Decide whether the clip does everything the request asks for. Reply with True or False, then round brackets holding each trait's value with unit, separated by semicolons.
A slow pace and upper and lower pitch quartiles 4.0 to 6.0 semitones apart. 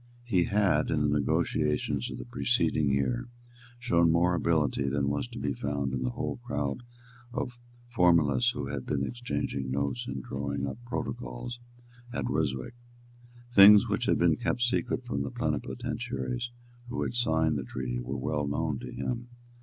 False (160 wpm; 4.9 semitones)